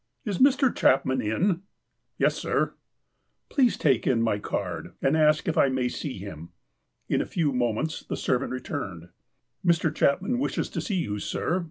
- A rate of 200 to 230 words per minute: No, average, 170 wpm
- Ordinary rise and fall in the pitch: No, wide, 6.7 semitones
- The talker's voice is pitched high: No, medium, 140 Hz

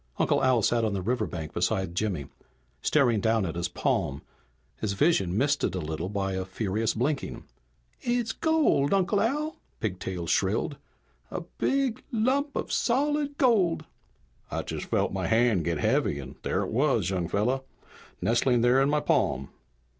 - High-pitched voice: No, low, 115 Hz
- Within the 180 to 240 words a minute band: No, average, 160 wpm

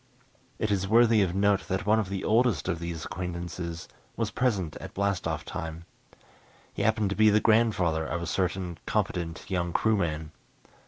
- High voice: No, very low, 95 Hz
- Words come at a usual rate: Yes, average, 170 wpm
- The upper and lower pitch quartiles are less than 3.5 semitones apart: No, average, 3.9 semitones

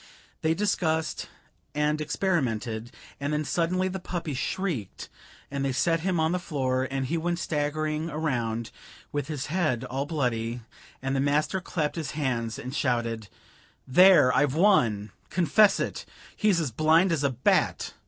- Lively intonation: No, average, 4.6 semitones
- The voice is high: No, medium, 150 Hz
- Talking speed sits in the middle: Yes, average, 155 wpm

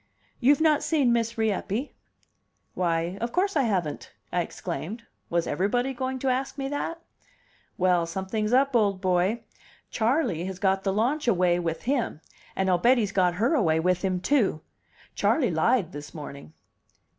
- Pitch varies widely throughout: Yes, wide, 6.3 semitones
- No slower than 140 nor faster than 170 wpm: Yes, average, 160 wpm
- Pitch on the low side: No, high, 205 Hz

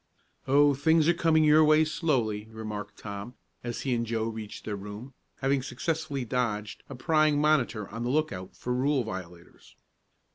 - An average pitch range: No, wide, 5.9 semitones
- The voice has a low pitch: Yes, low, 125 Hz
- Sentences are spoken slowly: No, average, 170 wpm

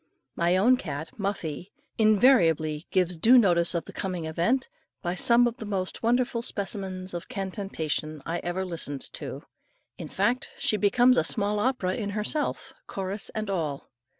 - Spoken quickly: No, average, 155 wpm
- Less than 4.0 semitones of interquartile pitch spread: No, average, 4.4 semitones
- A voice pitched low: No, high, 190 Hz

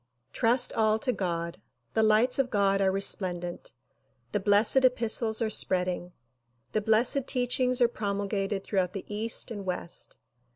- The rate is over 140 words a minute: Yes, average, 150 wpm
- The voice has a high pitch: Yes, high, 210 Hz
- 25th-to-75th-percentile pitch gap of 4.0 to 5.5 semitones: No, average, 3.3 semitones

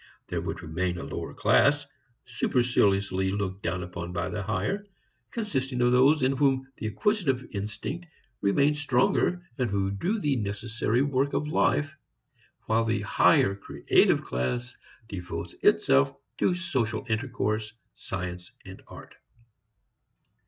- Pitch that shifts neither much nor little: No, wide, 6.0 semitones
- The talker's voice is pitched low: Yes, low, 115 Hz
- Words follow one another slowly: Yes, slow, 130 wpm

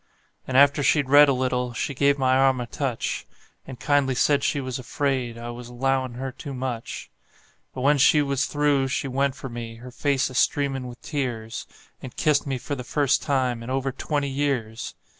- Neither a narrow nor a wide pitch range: No, narrow, 2.1 semitones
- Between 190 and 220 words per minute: Yes, average, 195 wpm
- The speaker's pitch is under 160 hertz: Yes, low, 135 Hz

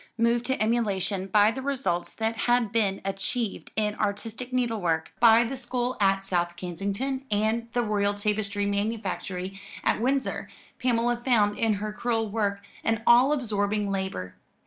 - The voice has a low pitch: No, high, 215 Hz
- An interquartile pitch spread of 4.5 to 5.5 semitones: No, average, 3.0 semitones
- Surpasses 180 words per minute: No, average, 150 wpm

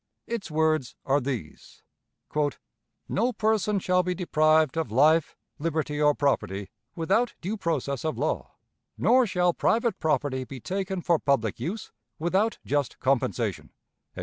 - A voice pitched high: No, medium, 160 Hz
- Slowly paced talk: Yes, slow, 130 wpm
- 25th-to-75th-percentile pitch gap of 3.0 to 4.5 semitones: No, average, 5.3 semitones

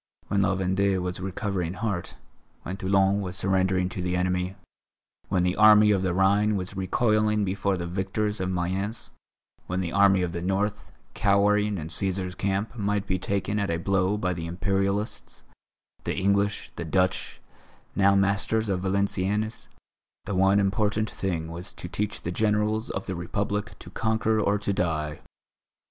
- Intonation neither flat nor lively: No, narrow, 2.1 semitones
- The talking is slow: No, average, 160 wpm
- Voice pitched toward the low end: Yes, very low, 95 Hz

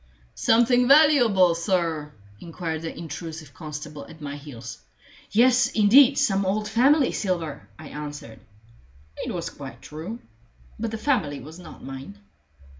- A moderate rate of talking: No, slow, 130 wpm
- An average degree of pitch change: No, wide, 7.3 semitones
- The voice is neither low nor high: Yes, medium, 170 Hz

